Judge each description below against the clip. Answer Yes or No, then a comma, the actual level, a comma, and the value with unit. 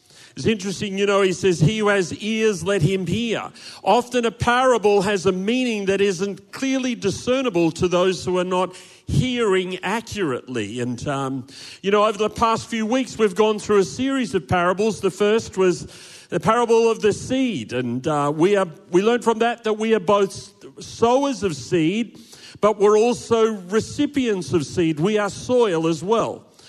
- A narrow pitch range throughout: No, average, 3.9 semitones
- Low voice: No, high, 205 Hz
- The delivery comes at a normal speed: Yes, average, 180 wpm